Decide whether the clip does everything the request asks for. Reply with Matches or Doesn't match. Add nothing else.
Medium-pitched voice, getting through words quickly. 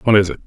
Doesn't match